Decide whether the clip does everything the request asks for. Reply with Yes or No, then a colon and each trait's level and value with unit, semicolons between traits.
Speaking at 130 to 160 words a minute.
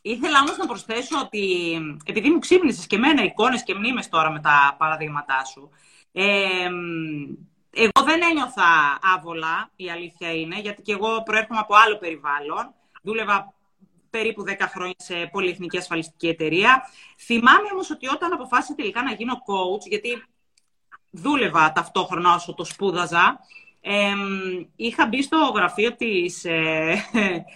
Yes: average, 140 wpm